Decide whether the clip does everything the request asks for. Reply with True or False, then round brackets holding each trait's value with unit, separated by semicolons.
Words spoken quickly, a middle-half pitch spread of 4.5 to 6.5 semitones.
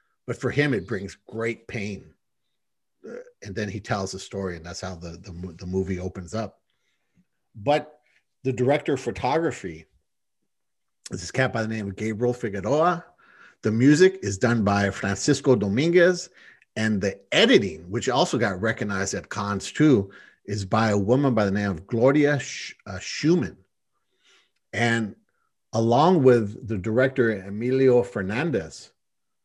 False (150 wpm; 4.9 semitones)